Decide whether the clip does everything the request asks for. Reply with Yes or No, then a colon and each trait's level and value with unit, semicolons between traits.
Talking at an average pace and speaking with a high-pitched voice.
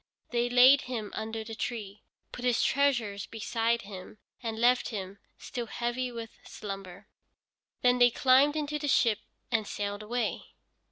Yes: average, 150 wpm; high, 235 Hz